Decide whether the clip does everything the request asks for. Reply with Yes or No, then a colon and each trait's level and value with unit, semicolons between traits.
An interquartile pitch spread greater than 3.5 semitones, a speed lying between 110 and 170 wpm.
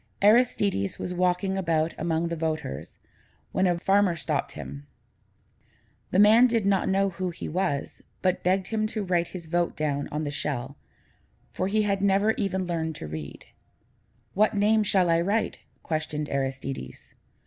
Yes: average, 4.3 semitones; average, 160 wpm